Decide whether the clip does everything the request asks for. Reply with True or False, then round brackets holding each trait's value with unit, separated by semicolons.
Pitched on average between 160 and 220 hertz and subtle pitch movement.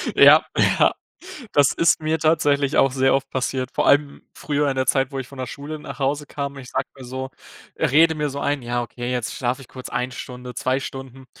False (135 Hz; 2.0 semitones)